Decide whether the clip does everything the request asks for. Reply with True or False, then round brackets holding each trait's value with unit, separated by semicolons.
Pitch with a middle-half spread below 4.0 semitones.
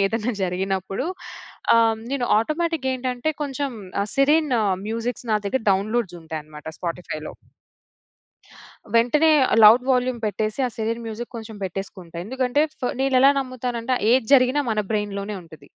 False (4.6 semitones)